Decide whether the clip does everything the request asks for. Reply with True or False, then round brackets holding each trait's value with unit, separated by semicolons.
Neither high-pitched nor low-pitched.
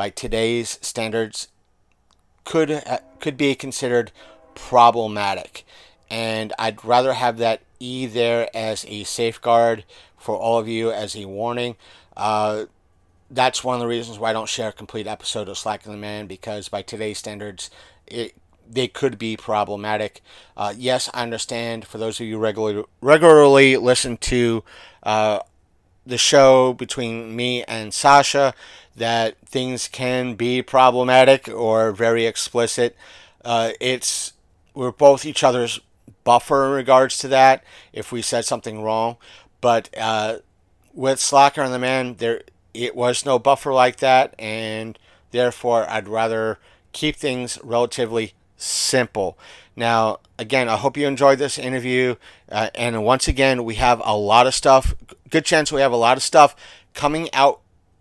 False (115 Hz)